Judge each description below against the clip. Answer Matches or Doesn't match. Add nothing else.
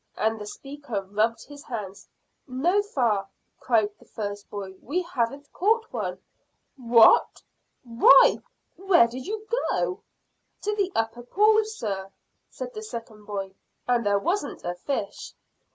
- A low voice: Doesn't match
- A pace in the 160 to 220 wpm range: Doesn't match